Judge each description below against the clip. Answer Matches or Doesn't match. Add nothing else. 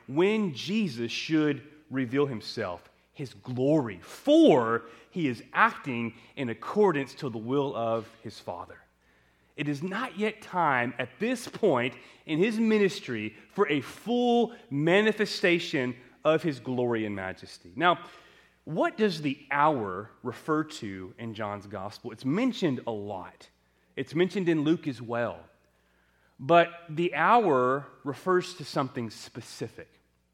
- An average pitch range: Doesn't match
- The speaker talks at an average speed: Doesn't match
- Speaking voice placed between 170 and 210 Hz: Doesn't match